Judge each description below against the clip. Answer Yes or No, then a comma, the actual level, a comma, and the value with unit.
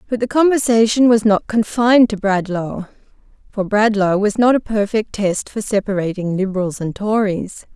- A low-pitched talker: No, high, 210 Hz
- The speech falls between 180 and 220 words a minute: No, average, 155 wpm